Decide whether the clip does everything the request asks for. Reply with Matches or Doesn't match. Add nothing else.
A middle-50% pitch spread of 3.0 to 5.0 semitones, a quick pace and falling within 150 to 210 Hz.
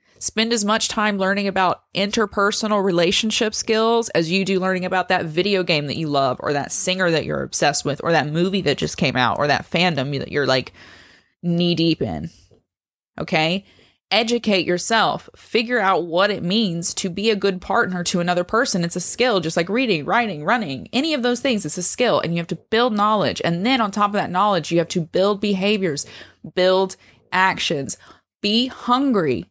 Doesn't match